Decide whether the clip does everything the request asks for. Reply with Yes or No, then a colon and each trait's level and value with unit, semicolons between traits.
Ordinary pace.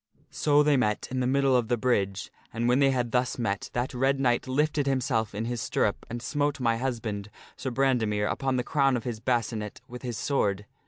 No: fast, 210 wpm